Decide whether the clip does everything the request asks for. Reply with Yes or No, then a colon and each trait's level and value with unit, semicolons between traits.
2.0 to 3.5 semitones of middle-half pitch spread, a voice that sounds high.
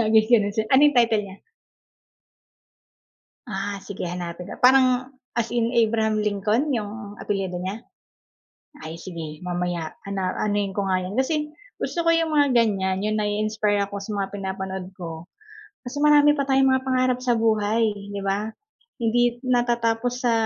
No: average, 3.9 semitones; high, 215 Hz